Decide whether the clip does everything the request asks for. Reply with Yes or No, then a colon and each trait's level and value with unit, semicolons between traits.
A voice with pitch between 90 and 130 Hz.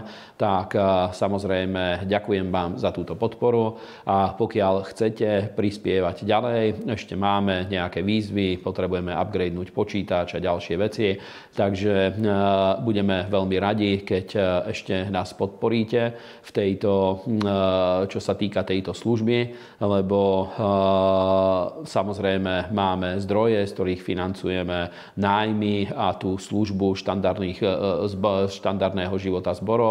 Yes: very low, 95 Hz